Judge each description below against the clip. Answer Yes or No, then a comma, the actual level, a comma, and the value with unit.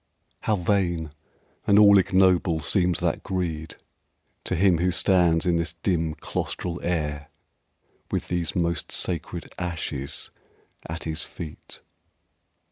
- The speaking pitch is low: Yes, very low, 85 Hz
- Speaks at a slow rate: Yes, slow, 120 wpm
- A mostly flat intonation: Yes, narrow, 2.2 semitones